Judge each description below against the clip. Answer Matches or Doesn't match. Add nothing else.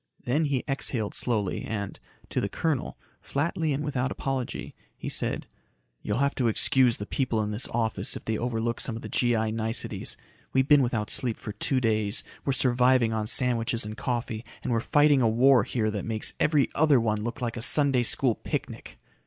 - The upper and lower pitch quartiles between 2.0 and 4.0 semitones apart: Matches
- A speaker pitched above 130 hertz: Doesn't match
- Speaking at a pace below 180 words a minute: Doesn't match